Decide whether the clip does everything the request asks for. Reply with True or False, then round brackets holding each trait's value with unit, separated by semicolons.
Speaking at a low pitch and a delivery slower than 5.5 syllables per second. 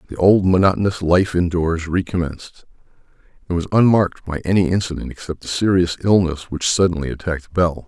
False (90 Hz; 5.8 syllables/s)